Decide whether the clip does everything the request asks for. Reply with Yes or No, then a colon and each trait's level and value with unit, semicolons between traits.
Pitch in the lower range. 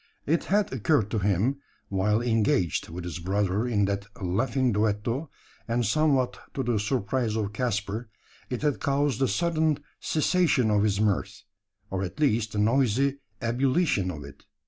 Yes: low, 115 Hz